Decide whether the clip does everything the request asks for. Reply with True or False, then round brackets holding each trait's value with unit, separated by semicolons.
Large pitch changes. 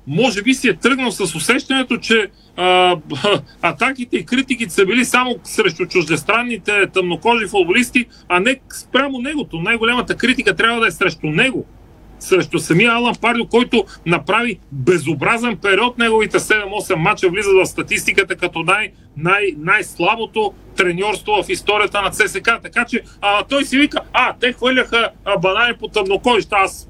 False (4.5 semitones)